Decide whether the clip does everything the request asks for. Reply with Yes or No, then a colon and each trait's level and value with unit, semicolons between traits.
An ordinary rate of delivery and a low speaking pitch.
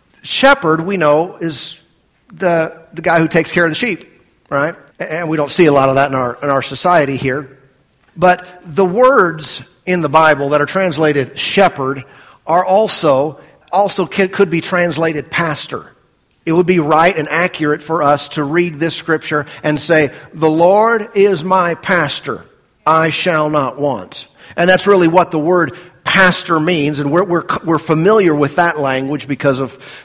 No: average, 170 wpm; medium, 160 Hz